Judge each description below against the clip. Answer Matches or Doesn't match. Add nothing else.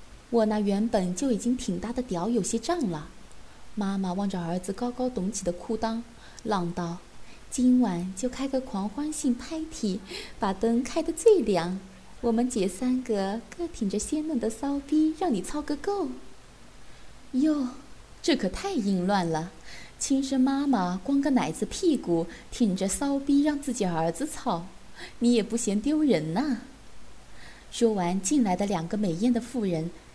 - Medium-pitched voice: Doesn't match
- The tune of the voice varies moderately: Doesn't match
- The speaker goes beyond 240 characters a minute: Doesn't match